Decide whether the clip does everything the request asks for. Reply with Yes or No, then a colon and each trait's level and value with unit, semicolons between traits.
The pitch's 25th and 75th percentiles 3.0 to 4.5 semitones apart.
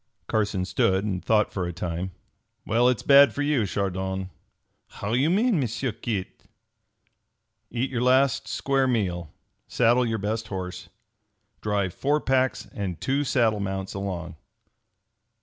No: average, 5.3 semitones